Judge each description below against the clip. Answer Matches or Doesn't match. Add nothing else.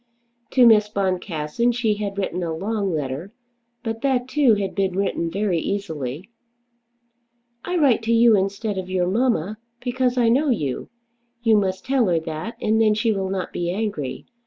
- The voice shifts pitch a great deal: Doesn't match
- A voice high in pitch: Matches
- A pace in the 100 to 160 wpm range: Doesn't match